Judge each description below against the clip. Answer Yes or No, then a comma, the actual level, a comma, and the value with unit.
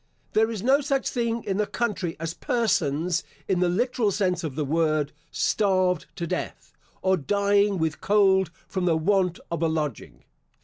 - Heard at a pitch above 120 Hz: Yes, medium, 185 Hz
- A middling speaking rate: Yes, average, 170 wpm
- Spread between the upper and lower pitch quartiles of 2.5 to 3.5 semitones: No, average, 4.2 semitones